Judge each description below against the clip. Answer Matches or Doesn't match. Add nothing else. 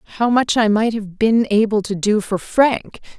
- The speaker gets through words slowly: Doesn't match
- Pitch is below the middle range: Doesn't match